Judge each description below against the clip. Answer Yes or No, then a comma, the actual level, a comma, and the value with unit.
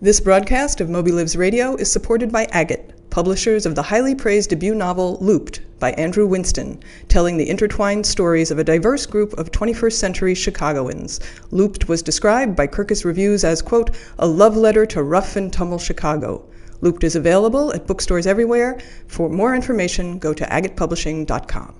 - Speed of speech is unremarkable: Yes, average, 170 wpm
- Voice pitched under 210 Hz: Yes, high, 190 Hz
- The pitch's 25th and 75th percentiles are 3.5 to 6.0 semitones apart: Yes, average, 4.4 semitones